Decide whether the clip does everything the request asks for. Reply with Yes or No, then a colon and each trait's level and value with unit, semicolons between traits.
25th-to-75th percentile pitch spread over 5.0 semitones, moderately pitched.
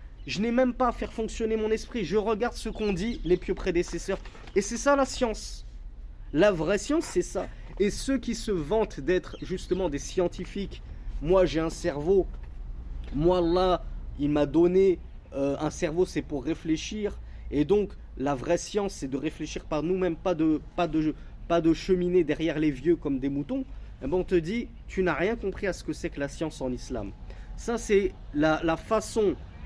Yes: wide, 5.4 semitones; medium, 175 Hz